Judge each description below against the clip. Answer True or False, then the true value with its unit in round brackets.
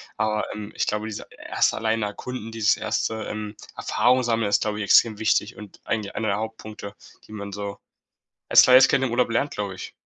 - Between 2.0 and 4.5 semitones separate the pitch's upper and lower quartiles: False (1.5 semitones)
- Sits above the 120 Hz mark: False (110 Hz)